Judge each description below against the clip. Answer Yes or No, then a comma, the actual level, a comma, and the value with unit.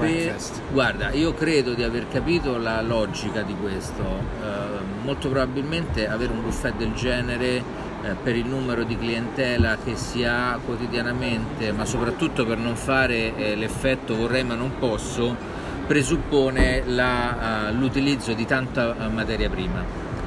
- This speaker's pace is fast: No, average, 140 wpm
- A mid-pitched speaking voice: No, low, 120 Hz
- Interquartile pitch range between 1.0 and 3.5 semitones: Yes, average, 2.7 semitones